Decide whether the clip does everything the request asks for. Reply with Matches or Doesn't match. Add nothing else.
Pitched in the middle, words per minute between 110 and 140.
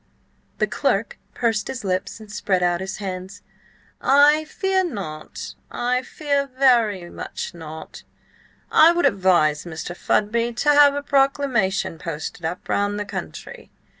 Doesn't match